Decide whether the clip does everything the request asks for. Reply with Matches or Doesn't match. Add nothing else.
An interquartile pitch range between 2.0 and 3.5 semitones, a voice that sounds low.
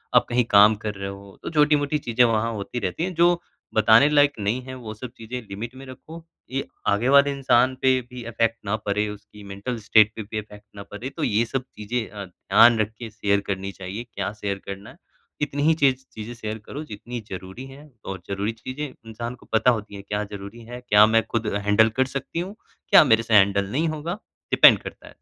Doesn't match